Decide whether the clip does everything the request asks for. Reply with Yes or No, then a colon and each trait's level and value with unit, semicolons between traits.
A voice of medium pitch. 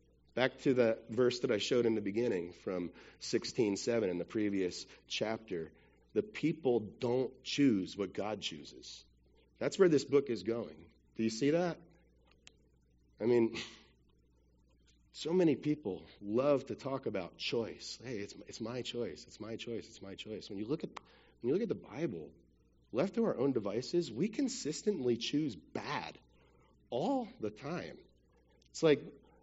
No: low, 115 Hz